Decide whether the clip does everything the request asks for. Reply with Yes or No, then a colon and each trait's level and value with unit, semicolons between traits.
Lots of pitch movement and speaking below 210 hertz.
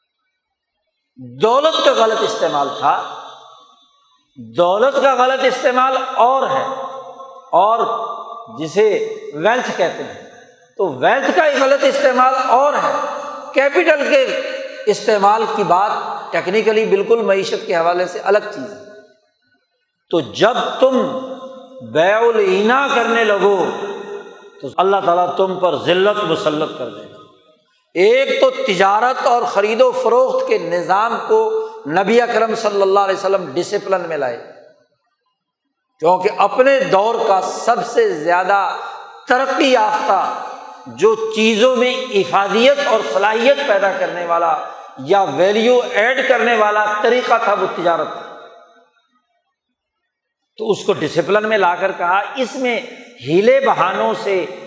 No: wide, 6.4 semitones; very high, 250 Hz